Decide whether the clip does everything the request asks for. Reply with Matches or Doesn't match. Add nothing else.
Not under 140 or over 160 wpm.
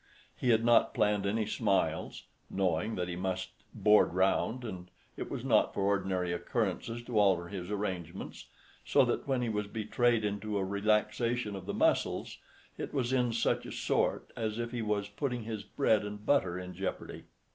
Doesn't match